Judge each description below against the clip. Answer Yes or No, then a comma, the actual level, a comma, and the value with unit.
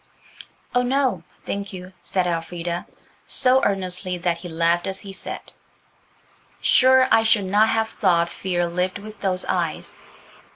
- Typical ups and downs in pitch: Yes, average, 3.6 semitones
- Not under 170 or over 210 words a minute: No, average, 140 wpm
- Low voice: No, medium, 185 Hz